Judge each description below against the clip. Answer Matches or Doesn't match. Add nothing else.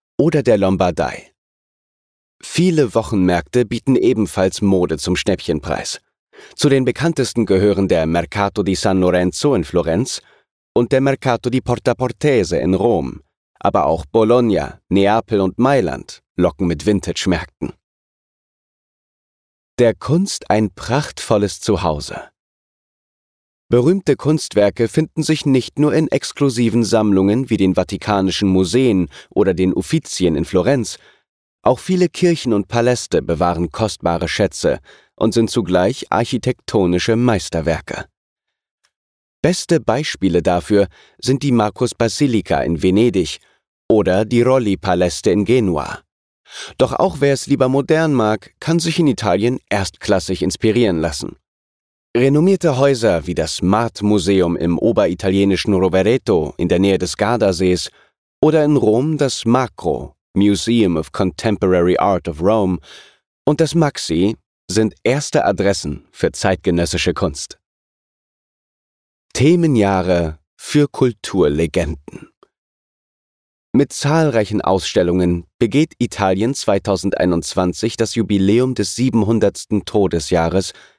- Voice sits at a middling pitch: Doesn't match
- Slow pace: Matches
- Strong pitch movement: Matches